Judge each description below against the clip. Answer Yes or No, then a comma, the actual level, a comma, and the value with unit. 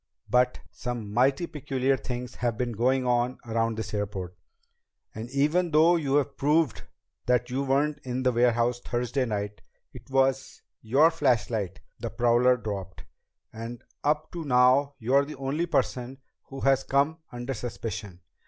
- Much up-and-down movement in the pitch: No, average, 2.8 semitones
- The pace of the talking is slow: No, average, 145 wpm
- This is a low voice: Yes, low, 125 Hz